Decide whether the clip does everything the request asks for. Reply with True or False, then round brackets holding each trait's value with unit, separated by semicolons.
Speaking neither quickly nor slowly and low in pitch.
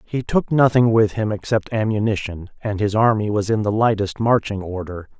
True (185 wpm; 105 Hz)